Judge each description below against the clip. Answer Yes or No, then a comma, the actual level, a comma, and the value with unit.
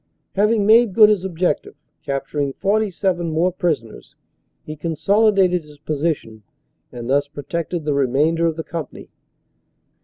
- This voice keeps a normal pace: No, slow, 125 wpm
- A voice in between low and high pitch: Yes, medium, 165 Hz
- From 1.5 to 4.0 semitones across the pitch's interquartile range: No, average, 4.8 semitones